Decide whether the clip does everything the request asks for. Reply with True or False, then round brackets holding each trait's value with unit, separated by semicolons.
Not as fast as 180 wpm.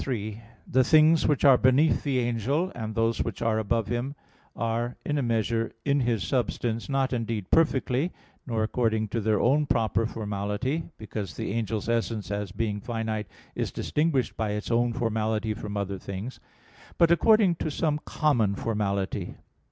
True (160 wpm)